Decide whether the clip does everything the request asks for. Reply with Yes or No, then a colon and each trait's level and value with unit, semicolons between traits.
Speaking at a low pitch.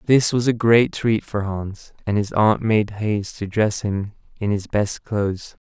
Yes: low, 105 Hz